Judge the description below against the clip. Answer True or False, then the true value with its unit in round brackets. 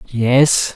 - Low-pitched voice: True (125 Hz)